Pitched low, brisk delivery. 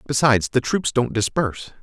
No: low, 125 Hz; average, 165 wpm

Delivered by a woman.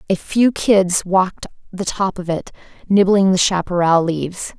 Yes: female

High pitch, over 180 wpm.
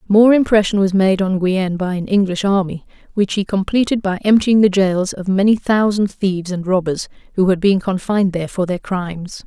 Yes: high, 195 Hz; average, 195 wpm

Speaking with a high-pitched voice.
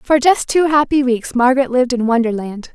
Yes: very high, 255 Hz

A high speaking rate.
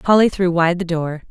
Yes: fast, 230 wpm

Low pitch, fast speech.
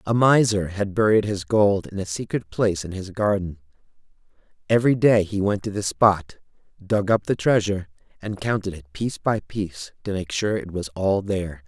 No: low, 100 Hz; average, 190 wpm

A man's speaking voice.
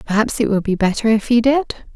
No: female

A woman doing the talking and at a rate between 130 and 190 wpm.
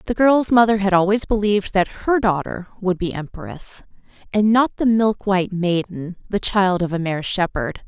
Yes: female; average, 175 wpm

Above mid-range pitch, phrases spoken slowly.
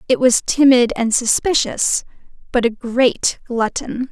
Yes: high, 245 Hz; slow, 130 wpm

